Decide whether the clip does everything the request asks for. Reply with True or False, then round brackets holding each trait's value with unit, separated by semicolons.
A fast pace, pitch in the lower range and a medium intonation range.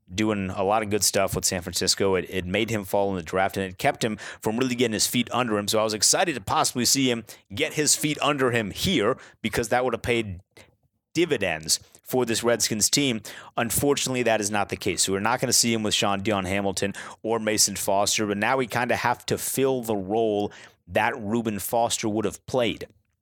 True (225 wpm; 110 Hz; 3.1 semitones)